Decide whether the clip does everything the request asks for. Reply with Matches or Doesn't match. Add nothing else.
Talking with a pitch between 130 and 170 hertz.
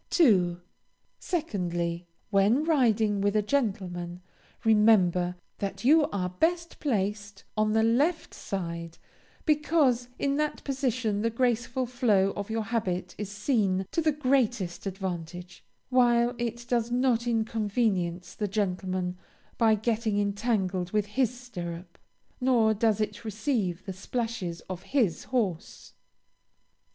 Doesn't match